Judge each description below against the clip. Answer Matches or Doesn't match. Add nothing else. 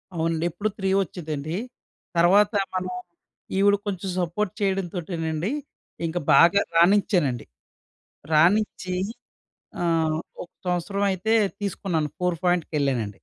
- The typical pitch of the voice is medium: Matches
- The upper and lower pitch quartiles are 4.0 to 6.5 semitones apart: Doesn't match